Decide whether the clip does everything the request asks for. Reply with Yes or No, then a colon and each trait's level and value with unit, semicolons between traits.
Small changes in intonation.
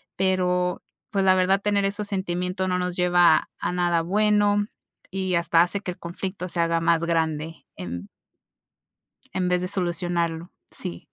Yes: narrow, 2.1 semitones